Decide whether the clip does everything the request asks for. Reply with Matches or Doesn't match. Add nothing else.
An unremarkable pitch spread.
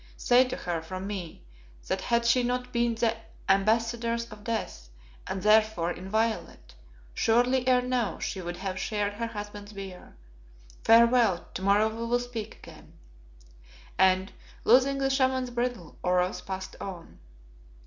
Matches